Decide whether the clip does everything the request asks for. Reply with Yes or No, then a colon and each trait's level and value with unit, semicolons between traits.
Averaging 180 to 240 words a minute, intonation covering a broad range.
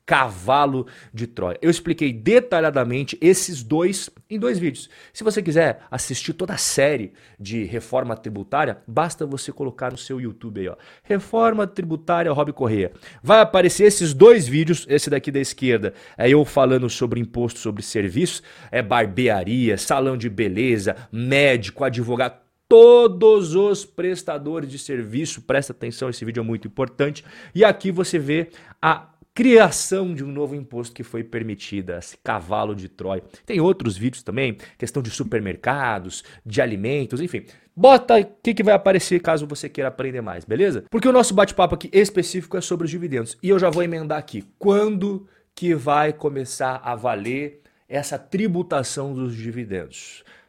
No: average, 155 wpm; wide, 6.6 semitones